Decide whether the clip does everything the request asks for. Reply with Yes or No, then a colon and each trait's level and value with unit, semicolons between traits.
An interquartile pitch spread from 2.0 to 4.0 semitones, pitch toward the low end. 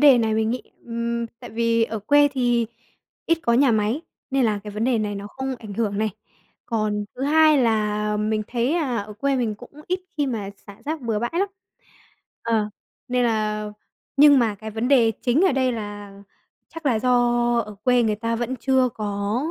No: average, 3.3 semitones; high, 230 Hz